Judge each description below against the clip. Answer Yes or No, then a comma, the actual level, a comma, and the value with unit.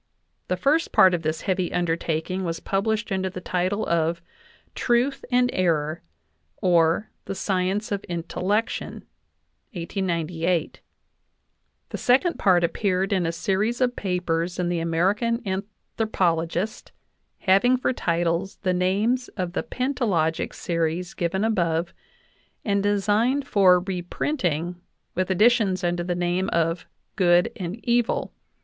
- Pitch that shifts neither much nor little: Yes, average, 3.4 semitones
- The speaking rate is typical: No, slow, 125 wpm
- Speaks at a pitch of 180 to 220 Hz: Yes, medium, 185 Hz